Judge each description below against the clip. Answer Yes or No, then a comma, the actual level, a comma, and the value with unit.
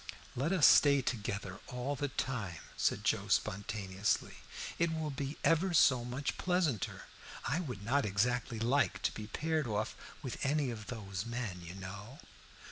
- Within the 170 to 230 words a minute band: No, average, 155 wpm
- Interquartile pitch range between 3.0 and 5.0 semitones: No, wide, 5.4 semitones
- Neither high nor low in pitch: No, low, 125 Hz